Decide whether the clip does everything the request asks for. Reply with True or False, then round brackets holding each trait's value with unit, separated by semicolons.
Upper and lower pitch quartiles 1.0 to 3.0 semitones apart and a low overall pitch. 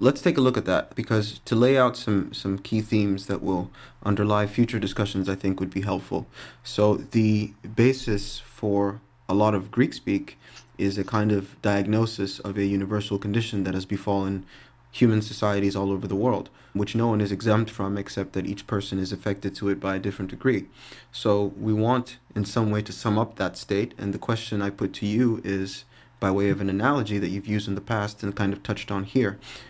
True (2.5 semitones; 105 Hz)